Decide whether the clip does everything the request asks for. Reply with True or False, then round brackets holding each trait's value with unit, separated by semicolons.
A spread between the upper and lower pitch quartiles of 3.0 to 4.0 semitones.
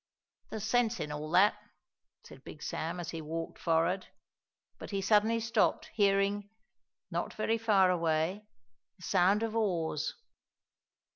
False (4.4 semitones)